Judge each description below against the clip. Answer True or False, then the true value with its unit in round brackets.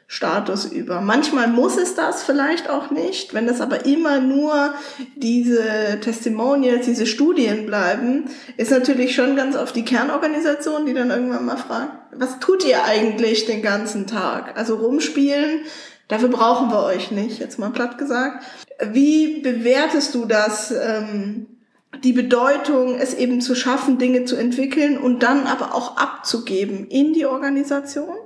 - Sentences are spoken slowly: False (150 wpm)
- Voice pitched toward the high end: True (255 Hz)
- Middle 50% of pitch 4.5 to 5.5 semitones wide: False (3.4 semitones)